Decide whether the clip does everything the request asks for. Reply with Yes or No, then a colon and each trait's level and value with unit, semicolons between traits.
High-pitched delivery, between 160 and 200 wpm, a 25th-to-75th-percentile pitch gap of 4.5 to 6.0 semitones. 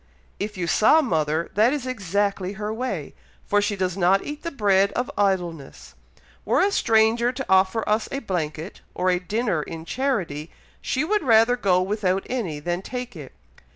Yes: high, 205 Hz; average, 175 wpm; average, 5.0 semitones